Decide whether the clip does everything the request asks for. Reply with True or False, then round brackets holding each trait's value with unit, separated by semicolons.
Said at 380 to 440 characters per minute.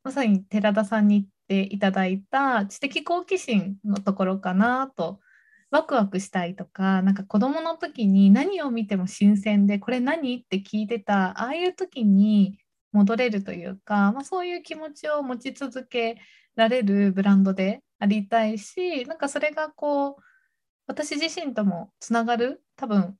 False (315 characters per minute)